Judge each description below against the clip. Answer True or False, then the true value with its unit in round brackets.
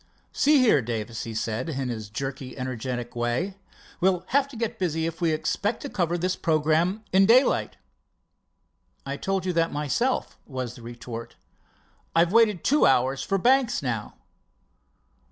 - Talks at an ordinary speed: True (155 wpm)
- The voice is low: False (160 Hz)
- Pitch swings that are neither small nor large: False (7.7 semitones)